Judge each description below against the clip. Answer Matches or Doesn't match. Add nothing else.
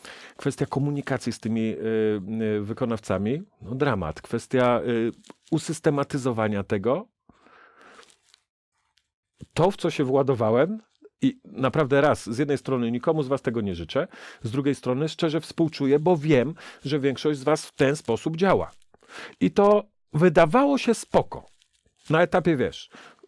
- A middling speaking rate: Matches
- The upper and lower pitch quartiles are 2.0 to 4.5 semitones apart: Doesn't match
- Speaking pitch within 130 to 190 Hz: Matches